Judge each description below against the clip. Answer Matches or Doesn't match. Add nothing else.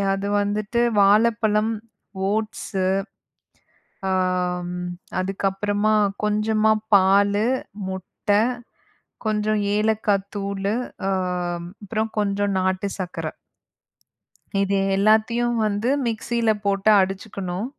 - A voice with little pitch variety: Matches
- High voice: Matches